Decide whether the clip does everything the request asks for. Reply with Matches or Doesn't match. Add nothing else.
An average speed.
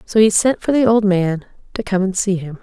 Doesn't match